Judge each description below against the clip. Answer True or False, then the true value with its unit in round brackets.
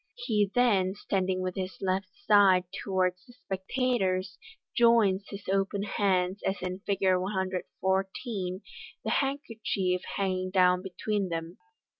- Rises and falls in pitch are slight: True (1.8 semitones)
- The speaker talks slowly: True (120 wpm)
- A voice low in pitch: False (190 Hz)